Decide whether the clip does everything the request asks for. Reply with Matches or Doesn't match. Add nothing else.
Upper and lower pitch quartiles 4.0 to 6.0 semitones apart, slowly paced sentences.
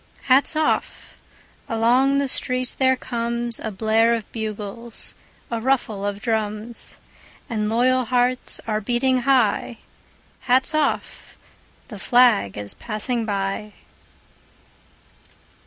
Doesn't match